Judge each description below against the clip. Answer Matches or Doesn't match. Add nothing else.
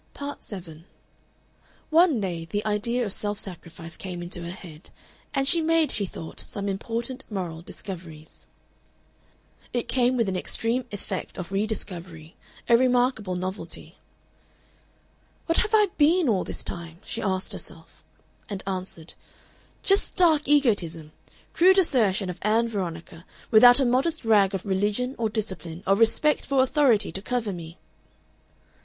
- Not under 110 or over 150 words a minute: Matches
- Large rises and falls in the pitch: Matches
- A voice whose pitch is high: Matches